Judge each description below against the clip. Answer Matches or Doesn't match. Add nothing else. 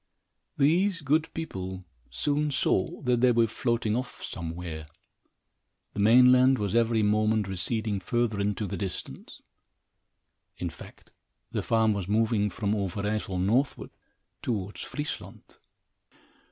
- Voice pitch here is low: Matches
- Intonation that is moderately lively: Matches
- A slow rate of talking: Matches